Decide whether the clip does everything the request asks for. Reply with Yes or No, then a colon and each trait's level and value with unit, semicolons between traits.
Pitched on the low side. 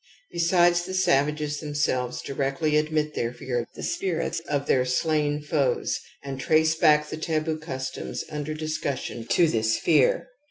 No: medium, 150 Hz